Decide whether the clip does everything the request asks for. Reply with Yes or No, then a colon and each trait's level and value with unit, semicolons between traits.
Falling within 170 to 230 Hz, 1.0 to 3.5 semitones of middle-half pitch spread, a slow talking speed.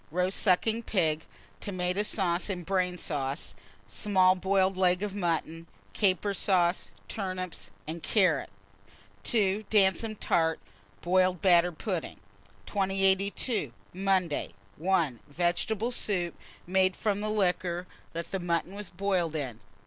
Yes: medium, 185 Hz; narrow, 2.4 semitones; slow, 110 wpm